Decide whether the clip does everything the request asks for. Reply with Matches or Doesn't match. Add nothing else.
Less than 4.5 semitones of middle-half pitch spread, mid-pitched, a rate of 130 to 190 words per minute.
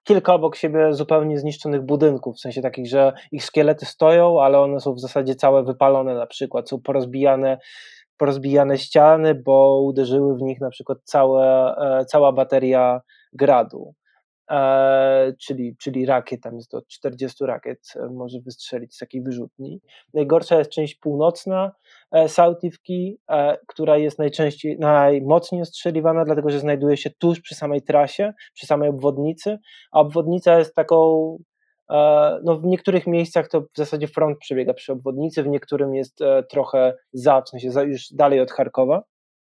Matches